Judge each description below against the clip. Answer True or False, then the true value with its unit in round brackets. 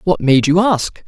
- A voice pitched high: False (170 Hz)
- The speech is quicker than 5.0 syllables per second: False (4.2 syllables/s)